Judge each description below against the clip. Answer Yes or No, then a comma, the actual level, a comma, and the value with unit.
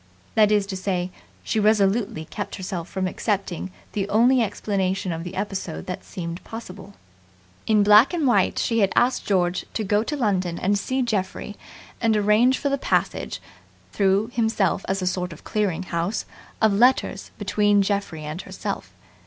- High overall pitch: Yes, high, 200 Hz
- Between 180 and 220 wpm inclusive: No, average, 165 wpm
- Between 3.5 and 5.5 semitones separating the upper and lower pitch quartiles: No, average, 2.7 semitones